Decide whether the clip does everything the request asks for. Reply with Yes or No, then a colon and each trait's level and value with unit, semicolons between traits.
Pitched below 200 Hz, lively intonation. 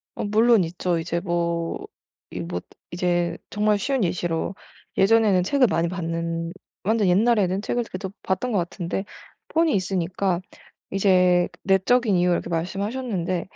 No: medium, 185 Hz; average, 3.3 semitones